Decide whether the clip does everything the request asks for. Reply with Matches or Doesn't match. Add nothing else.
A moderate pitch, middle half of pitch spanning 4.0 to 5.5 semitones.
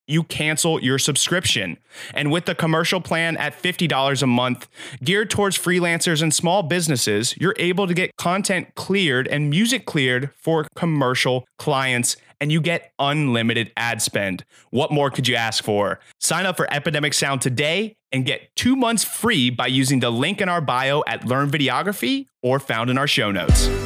Matches